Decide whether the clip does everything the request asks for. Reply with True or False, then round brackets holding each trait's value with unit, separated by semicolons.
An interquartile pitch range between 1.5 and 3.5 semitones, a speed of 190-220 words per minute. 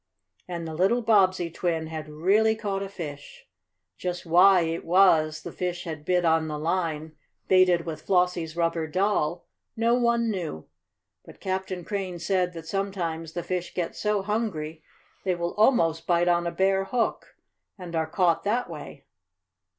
False (2.9 semitones; 160 wpm)